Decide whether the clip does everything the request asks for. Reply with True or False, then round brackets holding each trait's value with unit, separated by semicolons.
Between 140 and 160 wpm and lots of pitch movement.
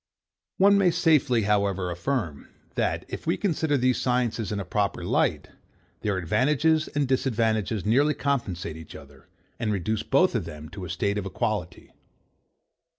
True (150 wpm; 6.8 semitones)